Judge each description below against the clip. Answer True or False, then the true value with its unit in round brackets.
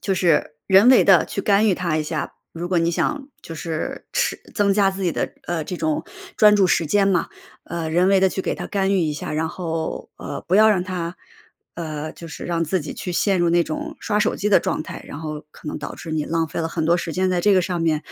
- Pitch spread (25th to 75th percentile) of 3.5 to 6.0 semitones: False (3.1 semitones)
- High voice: False (175 Hz)